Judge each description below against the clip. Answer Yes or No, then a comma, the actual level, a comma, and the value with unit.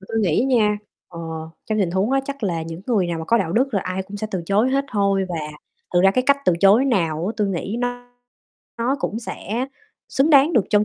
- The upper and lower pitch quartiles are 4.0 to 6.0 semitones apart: Yes, average, 4.6 semitones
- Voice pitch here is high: Yes, high, 210 Hz